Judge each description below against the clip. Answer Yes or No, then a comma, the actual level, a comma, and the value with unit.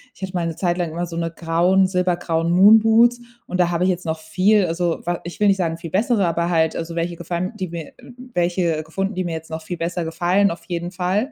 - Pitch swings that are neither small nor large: No, narrow, 1.9 semitones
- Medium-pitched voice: Yes, medium, 175 Hz